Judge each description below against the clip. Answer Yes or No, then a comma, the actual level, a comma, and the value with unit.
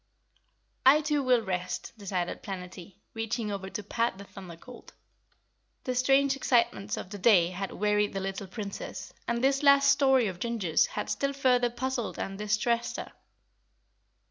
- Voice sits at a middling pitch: No, high, 225 Hz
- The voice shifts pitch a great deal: No, average, 4.8 semitones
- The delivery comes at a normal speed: Yes, average, 155 wpm